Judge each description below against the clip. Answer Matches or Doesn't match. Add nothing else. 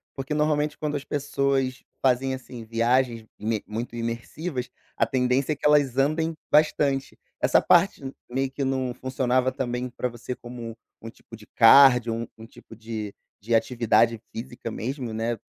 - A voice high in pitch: Doesn't match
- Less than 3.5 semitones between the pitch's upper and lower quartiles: Matches